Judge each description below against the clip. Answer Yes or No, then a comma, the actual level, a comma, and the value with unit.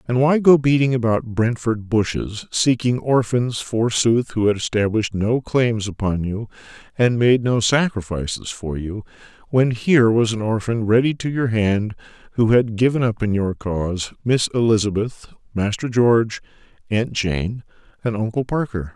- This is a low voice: Yes, low, 115 Hz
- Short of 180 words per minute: Yes, average, 150 wpm